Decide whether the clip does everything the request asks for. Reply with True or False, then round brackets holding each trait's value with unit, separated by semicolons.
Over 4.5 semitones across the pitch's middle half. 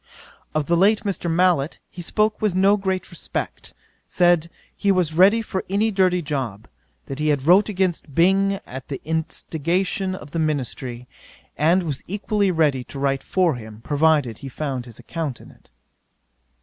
True (5.1 semitones)